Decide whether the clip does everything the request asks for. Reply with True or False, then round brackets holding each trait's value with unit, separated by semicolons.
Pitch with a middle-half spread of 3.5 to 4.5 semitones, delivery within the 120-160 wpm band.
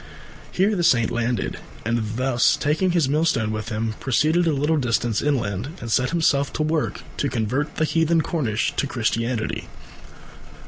False (5.4 semitones; 150 wpm)